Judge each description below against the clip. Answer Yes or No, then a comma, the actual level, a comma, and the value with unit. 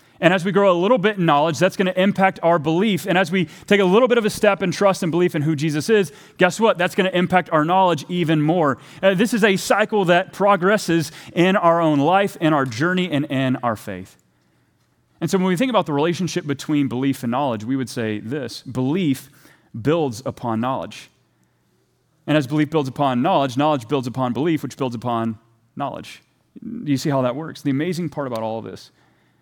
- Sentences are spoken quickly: Yes, fast, 220 wpm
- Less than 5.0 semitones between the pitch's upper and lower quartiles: No, wide, 5.5 semitones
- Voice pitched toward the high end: No, medium, 155 Hz